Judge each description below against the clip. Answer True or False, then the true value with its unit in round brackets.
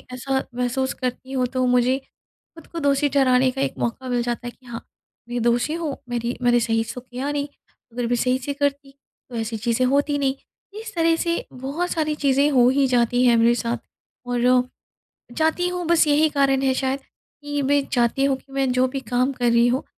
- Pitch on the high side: True (260 Hz)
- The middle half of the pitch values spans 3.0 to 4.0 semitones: False (2.6 semitones)